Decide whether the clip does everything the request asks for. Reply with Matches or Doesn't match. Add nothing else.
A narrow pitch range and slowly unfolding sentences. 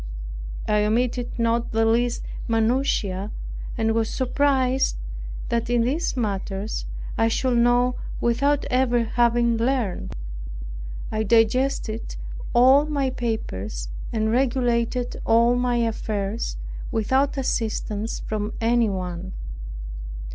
Matches